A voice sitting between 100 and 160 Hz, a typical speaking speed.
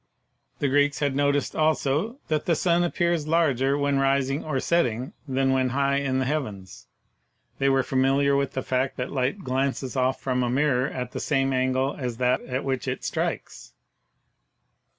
Yes: low, 135 Hz; average, 170 wpm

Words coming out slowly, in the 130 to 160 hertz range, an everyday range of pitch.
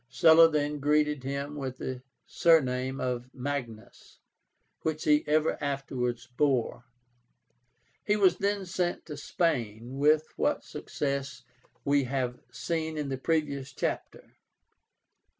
Yes: slow, 115 wpm; medium, 140 Hz; average, 3.2 semitones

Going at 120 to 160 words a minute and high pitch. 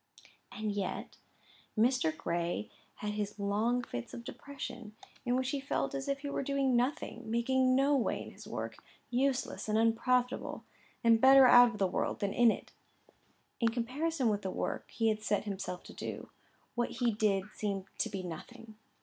No: average, 175 wpm; high, 230 Hz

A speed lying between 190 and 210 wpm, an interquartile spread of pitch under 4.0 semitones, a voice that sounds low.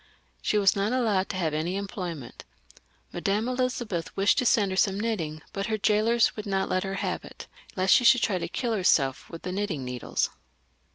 No: average, 195 wpm; average, 3.5 semitones; high, 195 Hz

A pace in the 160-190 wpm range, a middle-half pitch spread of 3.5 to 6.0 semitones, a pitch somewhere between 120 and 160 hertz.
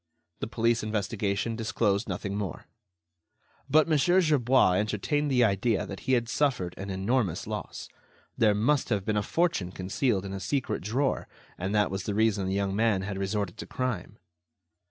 No: average, 170 wpm; average, 4.1 semitones; low, 105 Hz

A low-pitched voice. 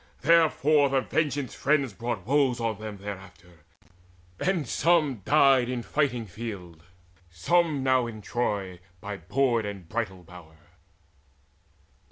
Yes: low, 120 Hz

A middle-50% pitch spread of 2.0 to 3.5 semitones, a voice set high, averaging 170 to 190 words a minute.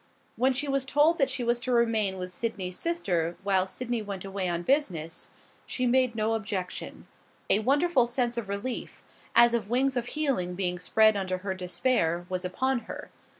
No: wide, 5.4 semitones; high, 225 Hz; average, 180 wpm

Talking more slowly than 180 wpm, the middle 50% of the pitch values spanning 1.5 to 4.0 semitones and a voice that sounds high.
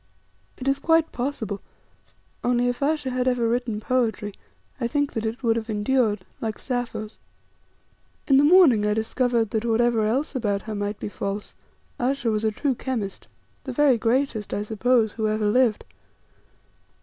Yes: average, 160 wpm; average, 3.2 semitones; high, 235 Hz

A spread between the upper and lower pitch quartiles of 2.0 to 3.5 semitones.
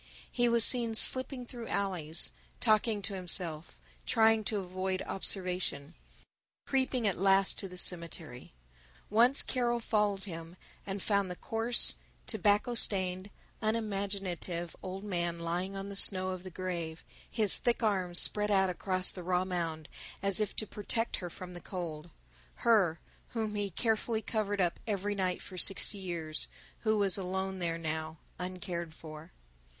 Yes: average, 3.2 semitones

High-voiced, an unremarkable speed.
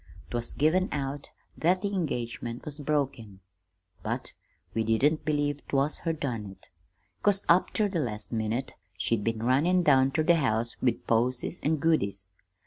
No: low, 135 Hz; average, 160 wpm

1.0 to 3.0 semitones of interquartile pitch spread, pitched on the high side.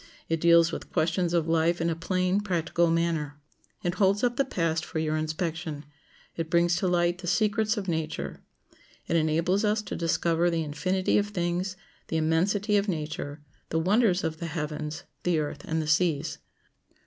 No: narrow, 2.6 semitones; medium, 170 Hz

